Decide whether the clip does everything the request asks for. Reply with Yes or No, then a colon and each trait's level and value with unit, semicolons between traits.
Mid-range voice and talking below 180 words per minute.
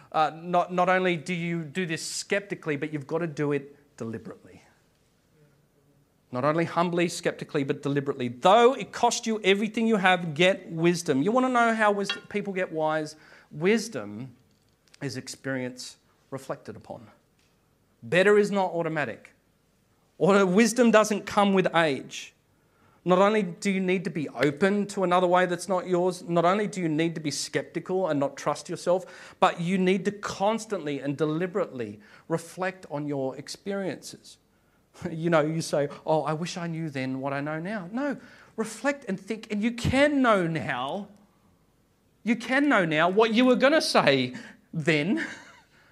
Yes: medium, 175 Hz; average, 165 wpm